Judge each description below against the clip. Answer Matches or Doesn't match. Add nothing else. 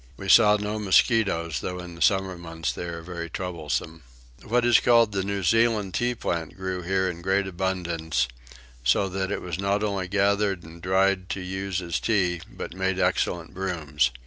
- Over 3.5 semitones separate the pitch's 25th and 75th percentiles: Doesn't match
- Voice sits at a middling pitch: Doesn't match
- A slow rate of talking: Doesn't match